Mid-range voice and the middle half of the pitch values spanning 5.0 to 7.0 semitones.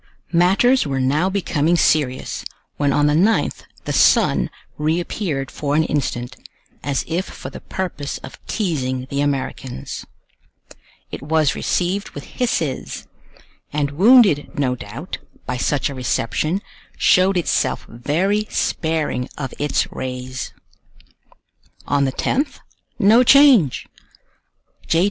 Yes: medium, 150 Hz; wide, 5.4 semitones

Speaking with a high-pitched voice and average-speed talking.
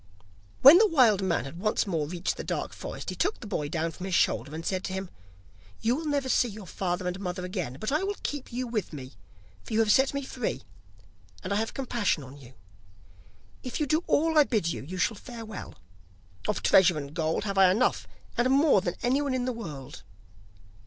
No: high, 205 Hz; fast, 220 wpm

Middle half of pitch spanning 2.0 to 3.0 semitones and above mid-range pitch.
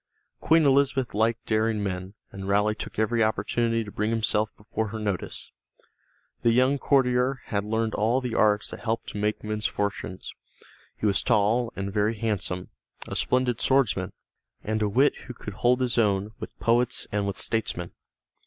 No: average, 2.7 semitones; low, 110 Hz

